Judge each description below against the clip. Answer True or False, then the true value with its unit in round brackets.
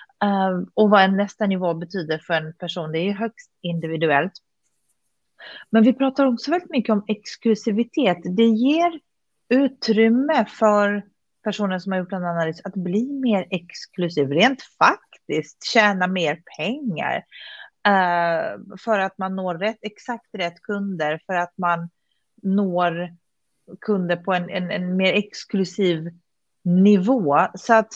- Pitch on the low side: False (200 Hz)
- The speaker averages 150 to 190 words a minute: False (135 wpm)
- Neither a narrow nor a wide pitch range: True (4.2 semitones)